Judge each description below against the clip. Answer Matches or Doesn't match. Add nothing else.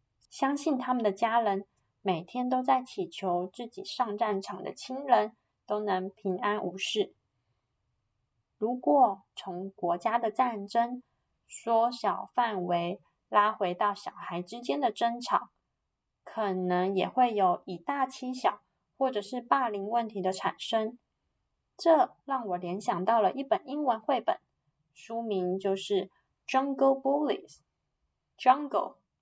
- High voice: Matches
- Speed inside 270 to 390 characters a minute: Doesn't match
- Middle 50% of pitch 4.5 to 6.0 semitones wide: Matches